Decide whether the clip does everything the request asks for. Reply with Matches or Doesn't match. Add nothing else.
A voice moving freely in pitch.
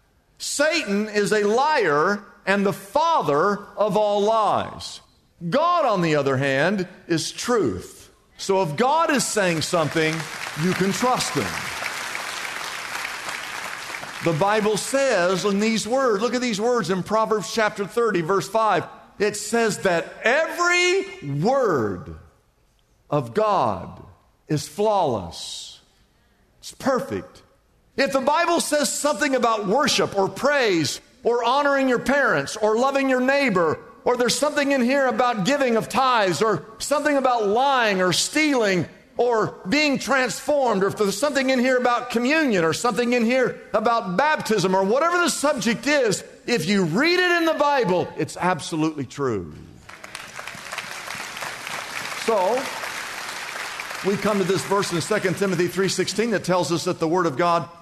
Matches